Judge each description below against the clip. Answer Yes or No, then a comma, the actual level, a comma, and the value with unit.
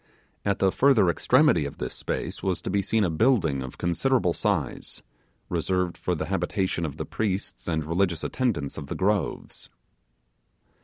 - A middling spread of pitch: Yes, average, 4.3 semitones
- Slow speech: No, average, 160 wpm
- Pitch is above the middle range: No, very low, 90 Hz